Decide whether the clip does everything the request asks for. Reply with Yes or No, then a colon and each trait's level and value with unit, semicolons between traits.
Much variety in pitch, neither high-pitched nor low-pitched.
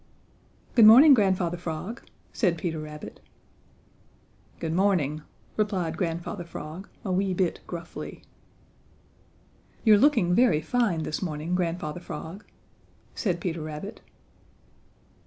No: average, 3.8 semitones; medium, 175 Hz